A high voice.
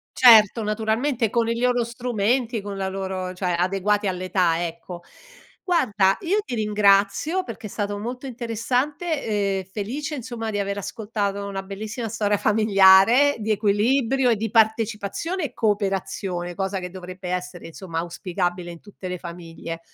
Yes: high, 205 Hz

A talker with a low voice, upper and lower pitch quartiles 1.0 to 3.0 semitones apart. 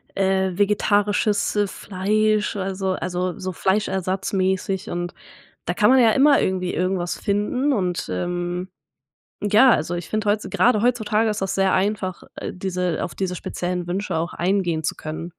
No: high, 190 Hz; narrow, 2.6 semitones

